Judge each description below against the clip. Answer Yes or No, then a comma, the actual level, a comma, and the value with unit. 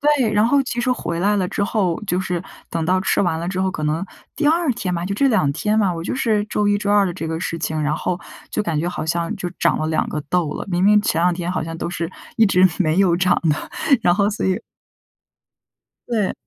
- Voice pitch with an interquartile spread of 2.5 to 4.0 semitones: Yes, average, 3.7 semitones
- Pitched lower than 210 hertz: Yes, medium, 185 Hz